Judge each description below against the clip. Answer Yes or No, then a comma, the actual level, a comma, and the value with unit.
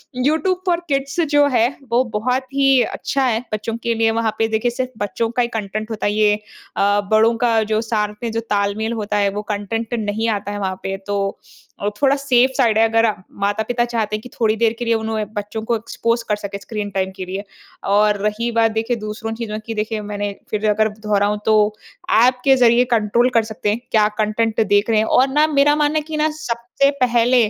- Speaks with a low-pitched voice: No, high, 225 Hz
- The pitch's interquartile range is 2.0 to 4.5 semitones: Yes, narrow, 2.5 semitones